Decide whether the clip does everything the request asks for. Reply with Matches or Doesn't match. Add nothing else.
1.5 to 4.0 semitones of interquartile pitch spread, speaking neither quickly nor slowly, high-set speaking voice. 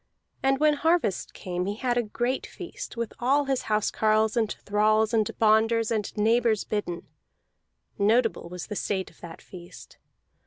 Matches